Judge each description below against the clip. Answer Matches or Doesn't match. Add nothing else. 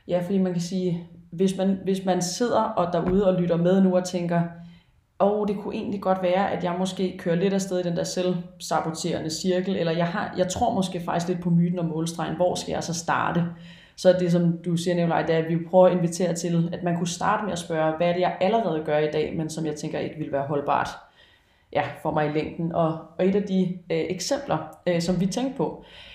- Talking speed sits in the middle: Doesn't match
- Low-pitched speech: Doesn't match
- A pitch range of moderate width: Doesn't match